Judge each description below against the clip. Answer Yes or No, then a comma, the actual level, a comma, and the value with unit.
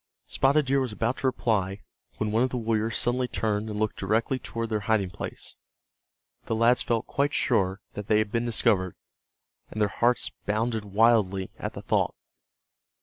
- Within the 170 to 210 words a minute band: Yes, average, 175 wpm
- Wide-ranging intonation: No, narrow, 2.6 semitones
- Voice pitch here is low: Yes, low, 110 Hz